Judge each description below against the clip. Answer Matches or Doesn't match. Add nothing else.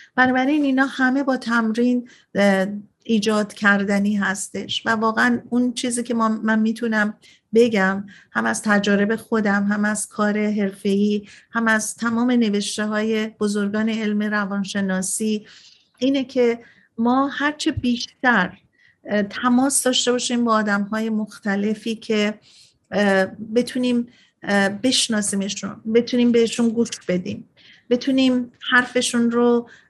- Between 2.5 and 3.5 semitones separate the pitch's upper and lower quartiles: Matches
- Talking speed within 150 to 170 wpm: Doesn't match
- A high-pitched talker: Matches